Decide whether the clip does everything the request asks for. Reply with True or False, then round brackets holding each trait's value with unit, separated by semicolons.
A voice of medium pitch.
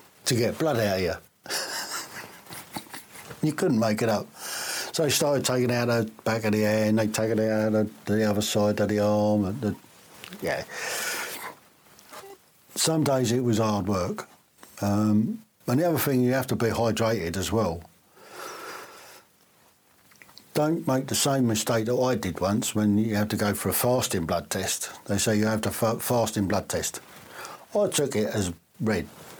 False (115 Hz)